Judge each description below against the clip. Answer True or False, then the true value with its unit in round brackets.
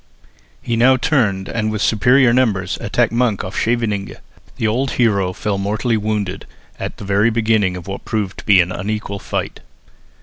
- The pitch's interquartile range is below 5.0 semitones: True (2.9 semitones)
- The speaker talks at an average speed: True (170 wpm)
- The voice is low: True (105 Hz)